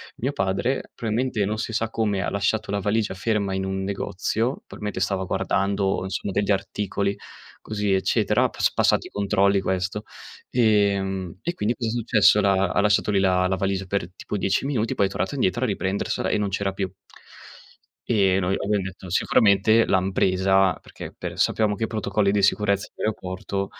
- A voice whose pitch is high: No, low, 100 Hz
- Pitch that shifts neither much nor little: No, narrow, 1.9 semitones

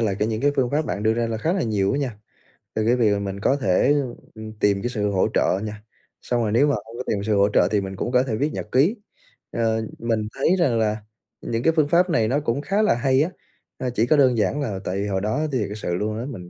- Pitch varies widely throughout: No, average, 4.3 semitones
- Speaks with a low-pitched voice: Yes, low, 115 Hz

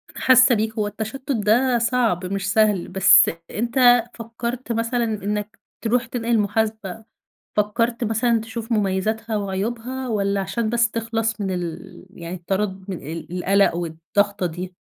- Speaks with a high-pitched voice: Yes, high, 215 Hz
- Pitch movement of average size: Yes, average, 3.2 semitones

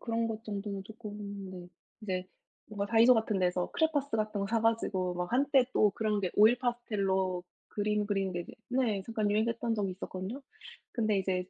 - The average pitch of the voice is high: Yes, high, 210 Hz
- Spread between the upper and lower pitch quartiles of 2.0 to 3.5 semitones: Yes, average, 3.1 semitones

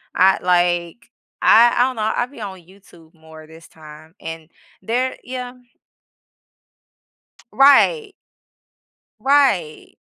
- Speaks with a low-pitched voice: No, high, 190 Hz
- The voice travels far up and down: Yes, wide, 7.4 semitones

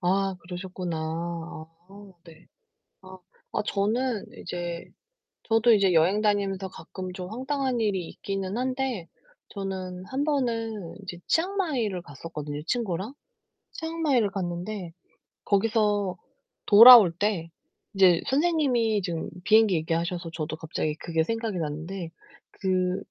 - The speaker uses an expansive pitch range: No, average, 4.6 semitones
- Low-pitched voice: No, high, 195 Hz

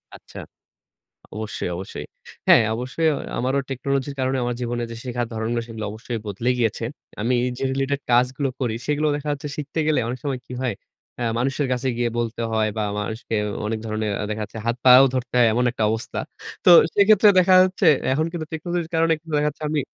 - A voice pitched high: No, low, 125 Hz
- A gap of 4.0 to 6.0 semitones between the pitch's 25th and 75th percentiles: Yes, average, 4.4 semitones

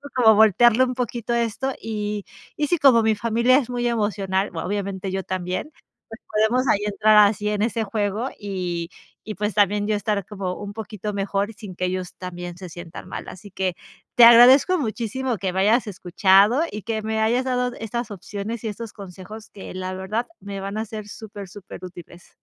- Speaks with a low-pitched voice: No, high, 210 Hz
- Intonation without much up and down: No, average, 3.2 semitones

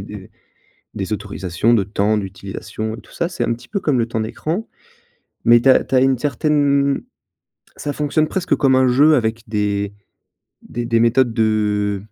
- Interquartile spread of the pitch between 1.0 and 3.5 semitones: No, average, 5.0 semitones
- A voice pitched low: Yes, low, 115 Hz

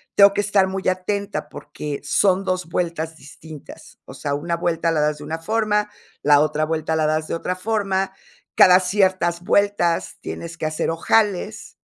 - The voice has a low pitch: No, medium, 175 Hz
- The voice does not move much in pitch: No, average, 3.7 semitones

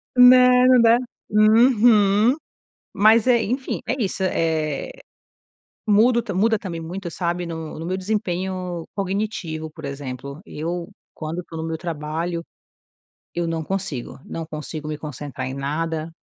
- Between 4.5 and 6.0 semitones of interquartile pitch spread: Yes, average, 5.1 semitones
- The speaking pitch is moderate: Yes, medium, 175 Hz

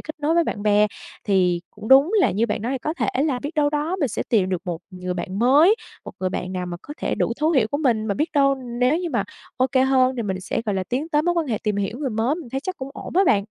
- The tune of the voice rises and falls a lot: Yes, wide, 6.4 semitones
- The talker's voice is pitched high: Yes, very high, 250 Hz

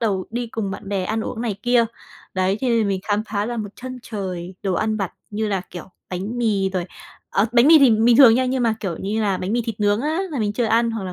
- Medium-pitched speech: No, high, 215 Hz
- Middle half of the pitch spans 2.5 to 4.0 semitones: Yes, average, 3.4 semitones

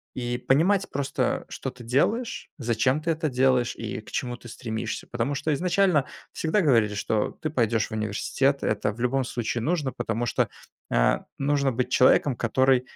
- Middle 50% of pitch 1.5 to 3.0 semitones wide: No, average, 3.7 semitones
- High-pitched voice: No, low, 130 Hz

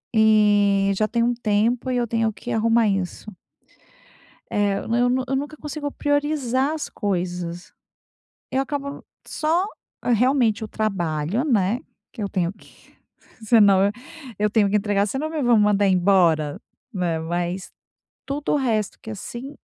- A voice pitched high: Yes, high, 220 Hz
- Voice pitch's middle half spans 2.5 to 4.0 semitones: No, average, 4.5 semitones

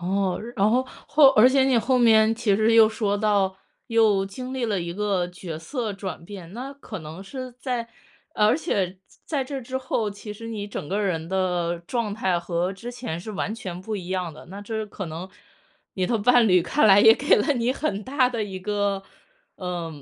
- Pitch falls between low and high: No, high, 205 Hz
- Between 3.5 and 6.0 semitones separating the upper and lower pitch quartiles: Yes, average, 4.1 semitones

